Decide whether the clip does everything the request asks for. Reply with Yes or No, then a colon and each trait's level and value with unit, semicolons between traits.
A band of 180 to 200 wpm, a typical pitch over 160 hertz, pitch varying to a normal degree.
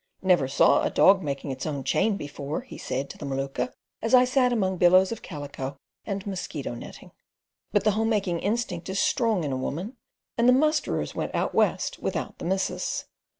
No: average, 190 wpm; high, 190 Hz; wide, 7.6 semitones